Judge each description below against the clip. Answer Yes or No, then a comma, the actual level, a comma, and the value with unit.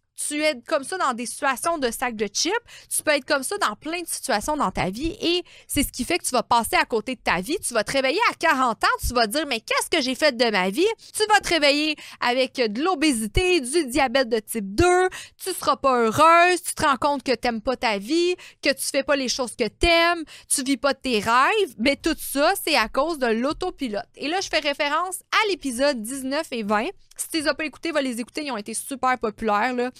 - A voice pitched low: No, very high, 280 Hz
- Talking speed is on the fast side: Yes, fast, 260 wpm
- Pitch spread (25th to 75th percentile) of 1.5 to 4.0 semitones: No, wide, 5.4 semitones